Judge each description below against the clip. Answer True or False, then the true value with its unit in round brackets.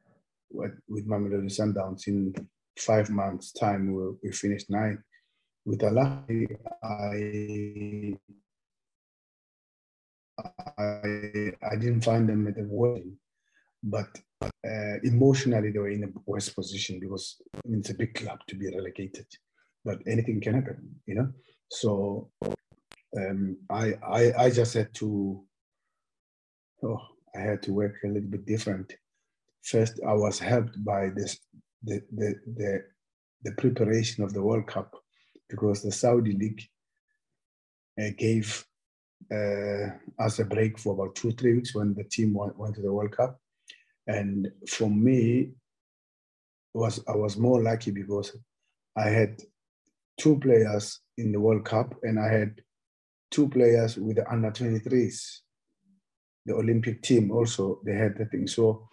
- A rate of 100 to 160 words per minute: True (140 wpm)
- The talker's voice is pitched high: False (105 Hz)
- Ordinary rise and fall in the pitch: False (2.3 semitones)